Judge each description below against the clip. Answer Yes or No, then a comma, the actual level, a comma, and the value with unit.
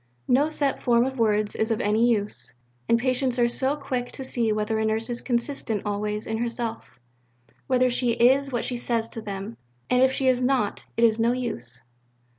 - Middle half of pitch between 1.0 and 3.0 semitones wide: Yes, narrow, 2.6 semitones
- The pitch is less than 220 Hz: No, high, 235 Hz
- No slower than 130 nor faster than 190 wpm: No, average, 200 wpm